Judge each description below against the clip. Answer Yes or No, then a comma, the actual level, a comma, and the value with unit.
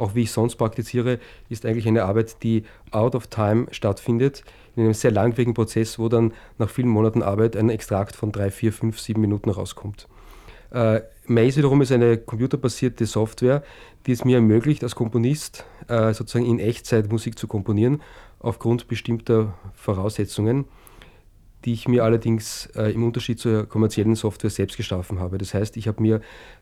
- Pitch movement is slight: Yes, narrow, 1.7 semitones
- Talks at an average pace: Yes, average, 170 wpm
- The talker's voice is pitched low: Yes, low, 115 Hz